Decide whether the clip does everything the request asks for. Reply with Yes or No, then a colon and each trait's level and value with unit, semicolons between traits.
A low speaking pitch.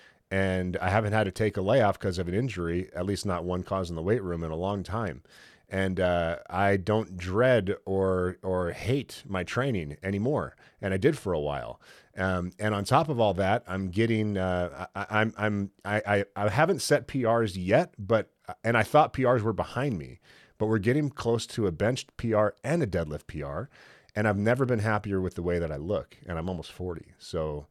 Yes: low, 100 Hz